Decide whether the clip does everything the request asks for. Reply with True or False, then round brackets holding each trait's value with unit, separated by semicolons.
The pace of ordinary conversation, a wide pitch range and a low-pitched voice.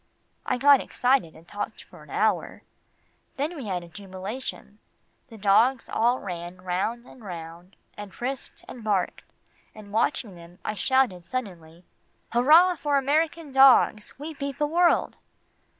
False (145 wpm; 6.7 semitones; 230 Hz)